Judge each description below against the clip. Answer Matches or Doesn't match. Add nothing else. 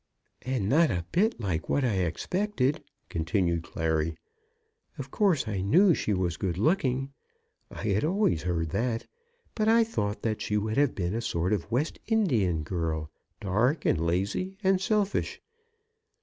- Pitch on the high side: Doesn't match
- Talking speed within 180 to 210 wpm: Doesn't match